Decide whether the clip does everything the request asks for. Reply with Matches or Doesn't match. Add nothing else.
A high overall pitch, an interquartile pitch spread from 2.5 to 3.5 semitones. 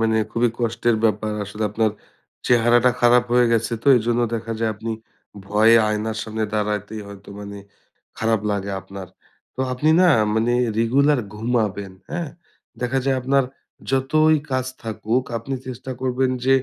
Doesn't match